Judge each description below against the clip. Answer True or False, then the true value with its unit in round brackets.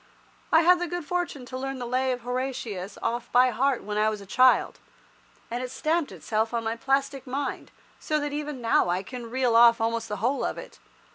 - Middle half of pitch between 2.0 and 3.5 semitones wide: True (3.2 semitones)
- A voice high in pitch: True (250 Hz)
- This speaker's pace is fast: True (215 wpm)